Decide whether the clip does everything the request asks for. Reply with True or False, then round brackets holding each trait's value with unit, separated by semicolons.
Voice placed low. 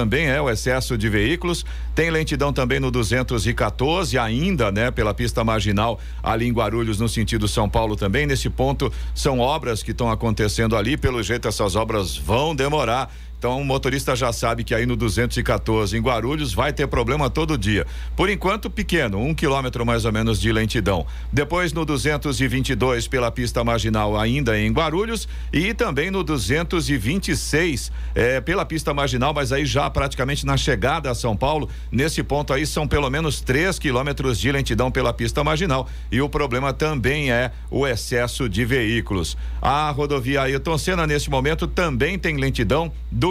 True (125 Hz)